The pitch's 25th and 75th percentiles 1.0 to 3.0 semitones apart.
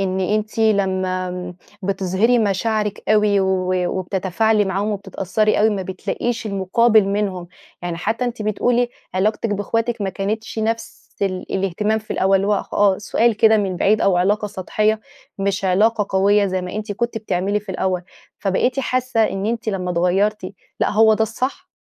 Yes: narrow, 2.5 semitones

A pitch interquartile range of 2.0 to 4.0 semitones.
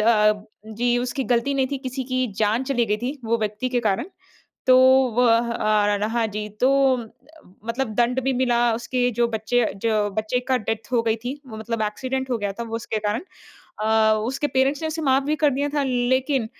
Yes: average, 3.2 semitones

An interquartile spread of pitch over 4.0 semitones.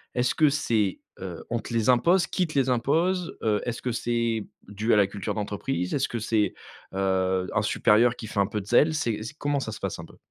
Yes: average, 4.6 semitones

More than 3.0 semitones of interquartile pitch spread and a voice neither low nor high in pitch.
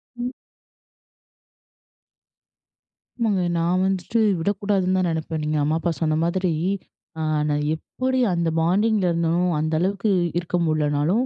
Yes: average, 3.8 semitones; medium, 175 Hz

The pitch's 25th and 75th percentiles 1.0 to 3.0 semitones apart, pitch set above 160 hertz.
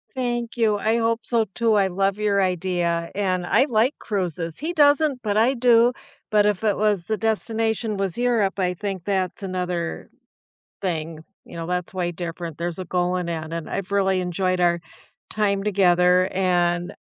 No: average, 3.7 semitones; high, 190 Hz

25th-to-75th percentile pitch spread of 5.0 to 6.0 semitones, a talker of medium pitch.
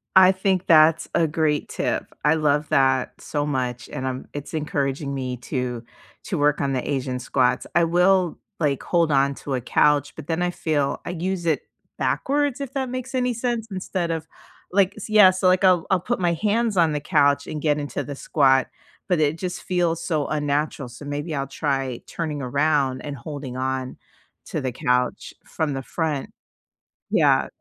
No: average, 4.4 semitones; medium, 150 Hz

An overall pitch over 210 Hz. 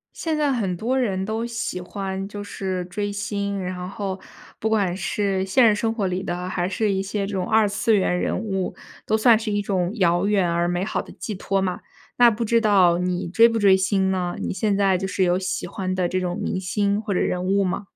No: high, 195 Hz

